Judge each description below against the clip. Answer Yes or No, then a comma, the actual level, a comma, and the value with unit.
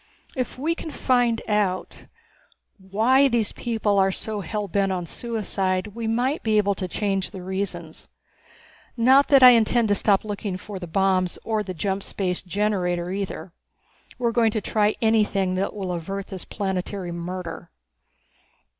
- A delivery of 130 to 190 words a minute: Yes, average, 160 wpm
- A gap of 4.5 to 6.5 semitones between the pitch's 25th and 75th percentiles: No, average, 3.2 semitones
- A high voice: Yes, high, 200 Hz